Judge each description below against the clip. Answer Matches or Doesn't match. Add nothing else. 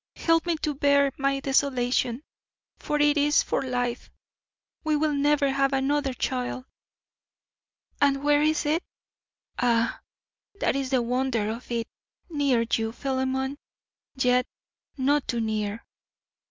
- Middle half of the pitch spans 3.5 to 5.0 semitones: Doesn't match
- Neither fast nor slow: Doesn't match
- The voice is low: Doesn't match